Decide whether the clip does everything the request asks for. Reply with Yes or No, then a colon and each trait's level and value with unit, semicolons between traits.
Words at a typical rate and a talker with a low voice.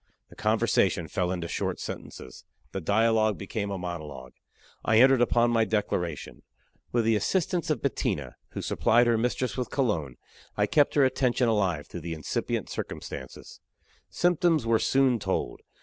Yes: average, 150 wpm; low, 110 Hz